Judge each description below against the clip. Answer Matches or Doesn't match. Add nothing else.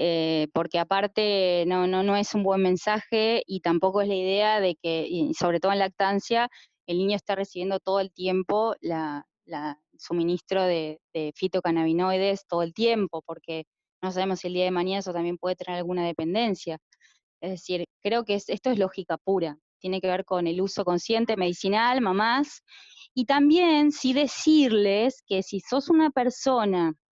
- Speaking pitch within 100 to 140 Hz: Doesn't match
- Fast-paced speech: Doesn't match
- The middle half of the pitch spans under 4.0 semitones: Matches